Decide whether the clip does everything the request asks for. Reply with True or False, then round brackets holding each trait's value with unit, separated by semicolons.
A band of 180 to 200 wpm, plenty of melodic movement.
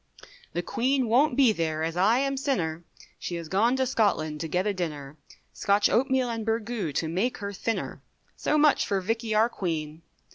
True (185 wpm; 6.5 semitones)